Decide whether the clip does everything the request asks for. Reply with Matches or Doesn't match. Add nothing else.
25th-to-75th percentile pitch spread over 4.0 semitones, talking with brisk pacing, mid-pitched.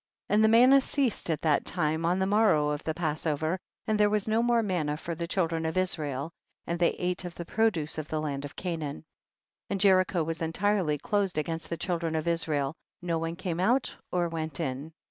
Doesn't match